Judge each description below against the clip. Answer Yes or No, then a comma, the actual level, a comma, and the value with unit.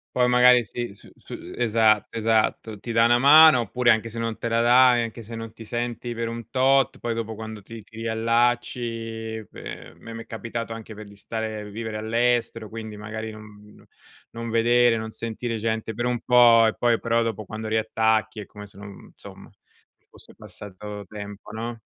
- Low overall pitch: Yes, low, 115 Hz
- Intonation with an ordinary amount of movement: No, narrow, 1.3 semitones